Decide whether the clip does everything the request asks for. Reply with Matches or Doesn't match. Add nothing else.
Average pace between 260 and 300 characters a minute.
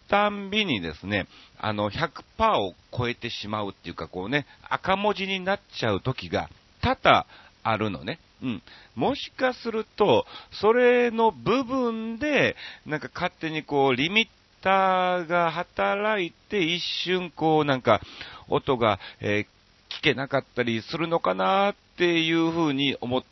Matches